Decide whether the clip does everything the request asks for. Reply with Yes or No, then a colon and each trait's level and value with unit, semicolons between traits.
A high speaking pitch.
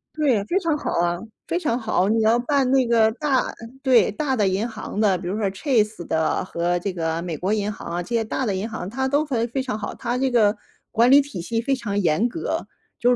Yes: high, 225 Hz